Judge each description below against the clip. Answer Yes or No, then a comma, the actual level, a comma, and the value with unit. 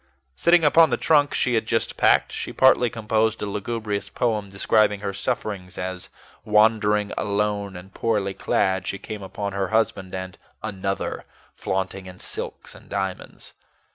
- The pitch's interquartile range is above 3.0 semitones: No, narrow, 2.4 semitones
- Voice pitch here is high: No, low, 105 Hz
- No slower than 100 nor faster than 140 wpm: No, average, 150 wpm